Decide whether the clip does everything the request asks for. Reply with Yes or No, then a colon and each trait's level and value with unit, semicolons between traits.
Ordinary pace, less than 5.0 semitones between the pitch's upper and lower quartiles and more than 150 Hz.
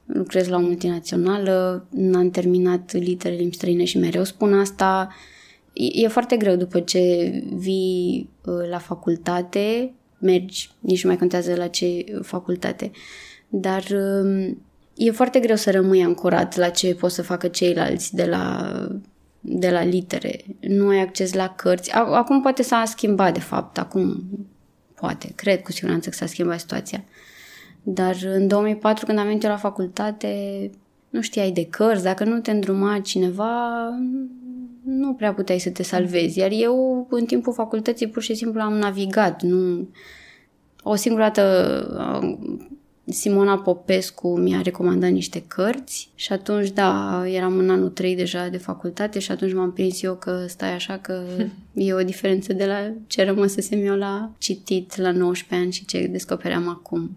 Yes: average, 155 wpm; average, 2.8 semitones; high, 190 Hz